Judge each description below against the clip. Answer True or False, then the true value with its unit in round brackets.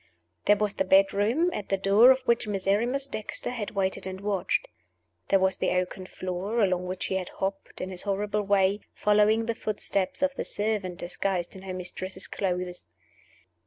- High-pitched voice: True (195 Hz)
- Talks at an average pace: True (175 wpm)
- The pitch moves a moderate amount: False (2.1 semitones)